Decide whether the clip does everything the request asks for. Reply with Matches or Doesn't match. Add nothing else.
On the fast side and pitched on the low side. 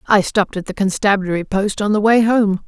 Doesn't match